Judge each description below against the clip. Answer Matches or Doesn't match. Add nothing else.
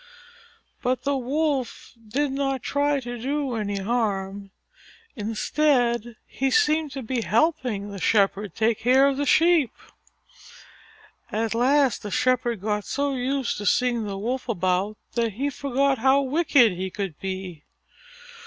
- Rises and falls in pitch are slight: Doesn't match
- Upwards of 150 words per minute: Doesn't match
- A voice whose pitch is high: Matches